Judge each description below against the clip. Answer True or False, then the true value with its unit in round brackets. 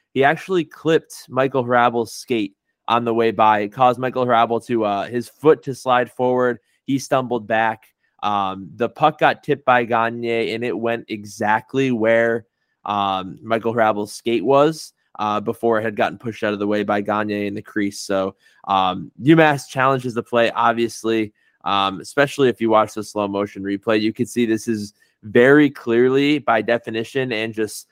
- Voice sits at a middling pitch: False (115 Hz)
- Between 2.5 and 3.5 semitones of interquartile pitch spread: True (3.0 semitones)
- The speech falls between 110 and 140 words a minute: False (180 wpm)